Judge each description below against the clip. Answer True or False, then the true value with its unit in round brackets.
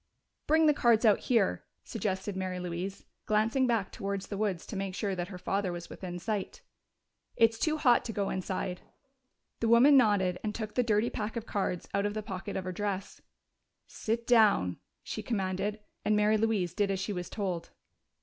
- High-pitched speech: True (205 Hz)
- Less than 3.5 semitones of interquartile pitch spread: True (3.1 semitones)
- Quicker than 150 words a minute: True (190 wpm)